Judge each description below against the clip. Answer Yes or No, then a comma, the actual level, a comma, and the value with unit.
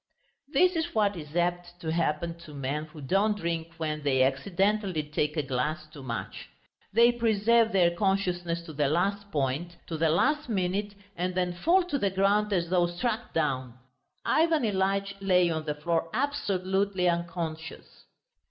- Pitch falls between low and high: Yes, medium, 175 Hz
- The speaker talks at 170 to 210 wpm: No, average, 160 wpm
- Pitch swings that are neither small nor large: Yes, average, 4.3 semitones